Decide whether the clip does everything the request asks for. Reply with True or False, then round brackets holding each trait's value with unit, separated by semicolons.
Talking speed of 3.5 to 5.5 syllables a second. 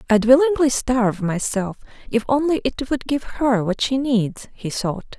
True (4.4 syllables/s)